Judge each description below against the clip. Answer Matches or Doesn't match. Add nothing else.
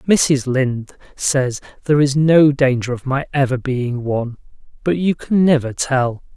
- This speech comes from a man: Matches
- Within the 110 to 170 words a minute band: Matches